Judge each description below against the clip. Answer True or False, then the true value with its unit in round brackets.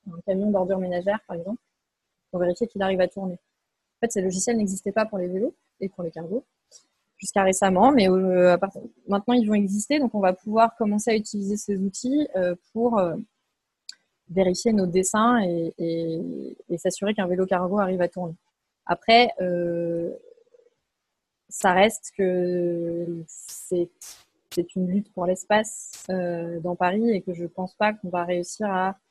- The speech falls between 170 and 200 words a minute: False (150 wpm)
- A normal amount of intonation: True (3.0 semitones)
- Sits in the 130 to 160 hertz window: False (190 Hz)